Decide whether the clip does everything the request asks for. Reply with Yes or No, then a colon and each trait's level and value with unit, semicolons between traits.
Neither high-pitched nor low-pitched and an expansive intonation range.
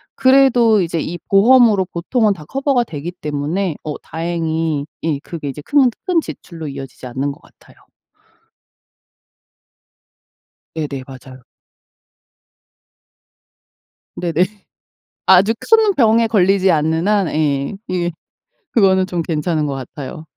Yes: medium, 170 Hz; wide, 5.8 semitones